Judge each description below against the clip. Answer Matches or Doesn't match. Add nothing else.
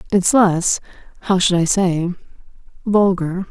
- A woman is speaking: Matches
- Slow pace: Matches